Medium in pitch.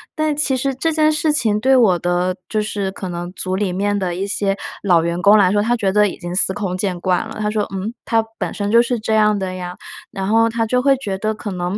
No: high, 205 Hz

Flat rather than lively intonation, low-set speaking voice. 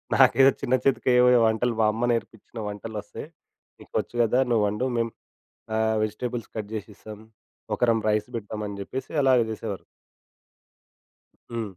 Yes: narrow, 2.3 semitones; low, 110 Hz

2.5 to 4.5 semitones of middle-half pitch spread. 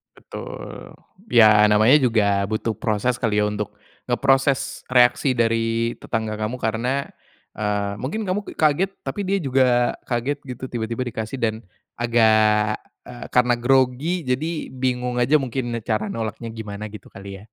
Yes: average, 3.2 semitones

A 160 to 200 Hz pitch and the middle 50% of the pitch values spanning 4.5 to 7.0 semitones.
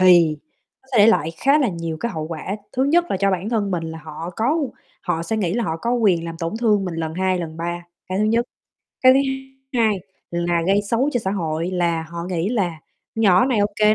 Yes: high, 190 Hz; average, 5.2 semitones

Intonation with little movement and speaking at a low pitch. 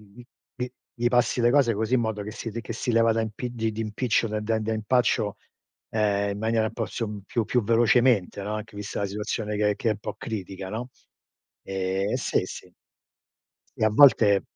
Yes: narrow, 2.1 semitones; low, 110 Hz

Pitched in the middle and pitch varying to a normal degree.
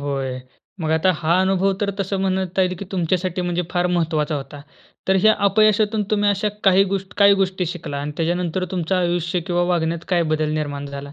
Yes: medium, 180 Hz; average, 3.2 semitones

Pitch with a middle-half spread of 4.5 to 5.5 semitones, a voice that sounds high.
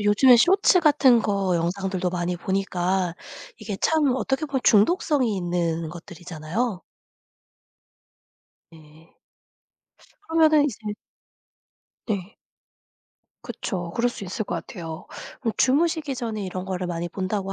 No: wide, 6.4 semitones; high, 195 Hz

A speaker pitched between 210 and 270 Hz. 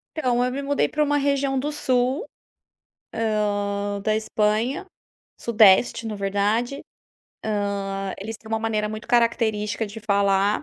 Yes: high, 220 Hz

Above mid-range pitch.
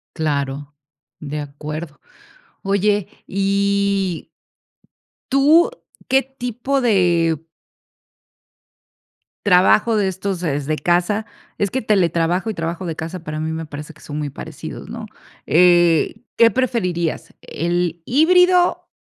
No: medium, 180 Hz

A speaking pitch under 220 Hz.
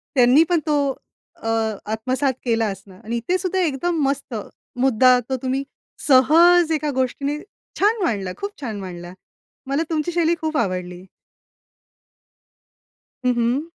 No: very high, 265 Hz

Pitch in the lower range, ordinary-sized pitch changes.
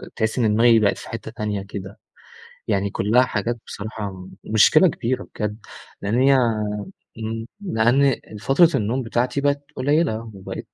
Yes: low, 115 Hz; average, 3.5 semitones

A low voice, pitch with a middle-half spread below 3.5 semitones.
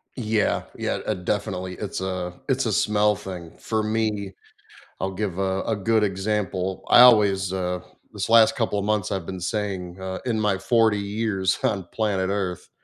Yes: low, 100 Hz; narrow, 2.4 semitones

